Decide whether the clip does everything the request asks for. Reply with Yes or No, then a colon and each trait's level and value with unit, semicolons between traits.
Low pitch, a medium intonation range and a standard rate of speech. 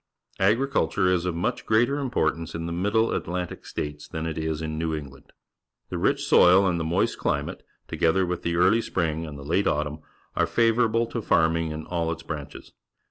Yes: very low, 85 Hz; average, 4.1 semitones; average, 190 wpm